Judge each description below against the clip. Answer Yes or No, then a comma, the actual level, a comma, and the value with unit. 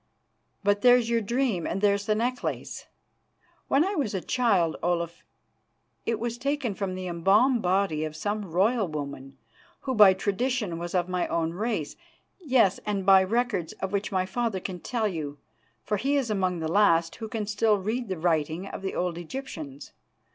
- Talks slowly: No, average, 175 wpm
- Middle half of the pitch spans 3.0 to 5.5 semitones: Yes, average, 5.0 semitones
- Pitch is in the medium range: No, high, 200 Hz